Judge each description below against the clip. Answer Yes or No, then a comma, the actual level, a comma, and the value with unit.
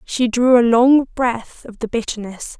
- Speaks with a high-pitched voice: Yes, high, 235 Hz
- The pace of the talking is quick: No, average, 185 wpm